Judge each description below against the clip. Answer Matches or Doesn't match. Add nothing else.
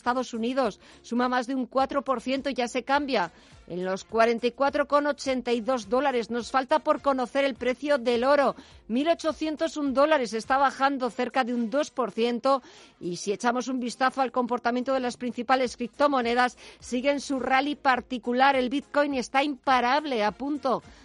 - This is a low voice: Doesn't match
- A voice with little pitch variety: Matches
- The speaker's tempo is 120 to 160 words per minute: Matches